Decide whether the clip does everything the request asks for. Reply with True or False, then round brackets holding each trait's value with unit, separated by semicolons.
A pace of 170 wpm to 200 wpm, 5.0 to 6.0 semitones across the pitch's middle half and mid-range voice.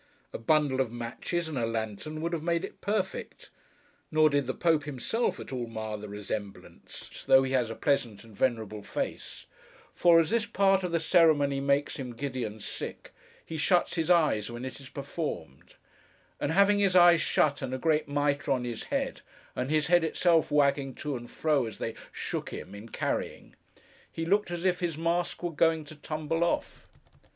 True (190 wpm; 5.3 semitones; 145 Hz)